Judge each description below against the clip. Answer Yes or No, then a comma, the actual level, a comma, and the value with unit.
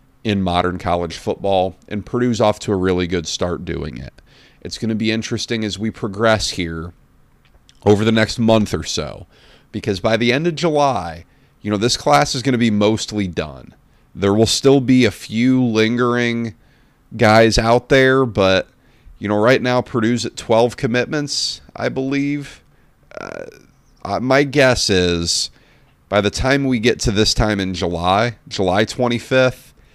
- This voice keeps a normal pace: Yes, average, 165 wpm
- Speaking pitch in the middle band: No, low, 110 Hz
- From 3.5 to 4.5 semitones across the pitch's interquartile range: Yes, average, 4.0 semitones